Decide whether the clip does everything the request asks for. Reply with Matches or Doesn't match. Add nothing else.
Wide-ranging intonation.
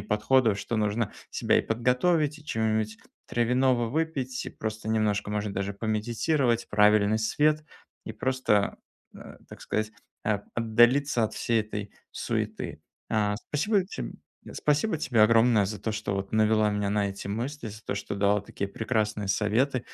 Doesn't match